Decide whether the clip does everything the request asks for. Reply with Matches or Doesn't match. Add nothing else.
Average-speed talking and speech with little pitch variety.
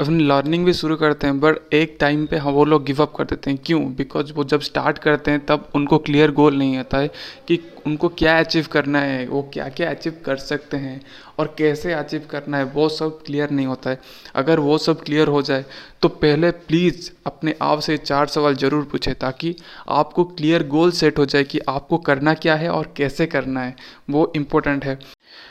Doesn't match